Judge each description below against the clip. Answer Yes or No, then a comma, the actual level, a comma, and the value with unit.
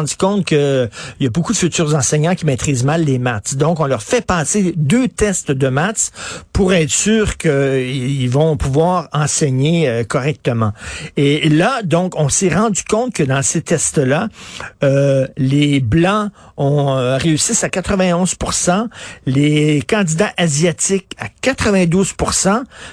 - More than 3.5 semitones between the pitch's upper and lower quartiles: Yes, average, 4.8 semitones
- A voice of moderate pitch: Yes, medium, 160 Hz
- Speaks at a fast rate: No, slow, 145 wpm